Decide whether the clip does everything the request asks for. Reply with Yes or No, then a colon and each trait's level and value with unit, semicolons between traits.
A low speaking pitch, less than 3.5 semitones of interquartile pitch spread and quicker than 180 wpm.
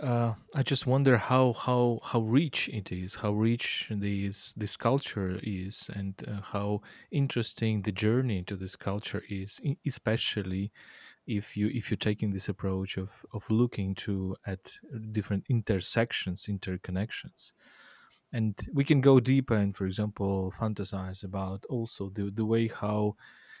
No: low, 105 Hz; average, 3.0 semitones; average, 145 wpm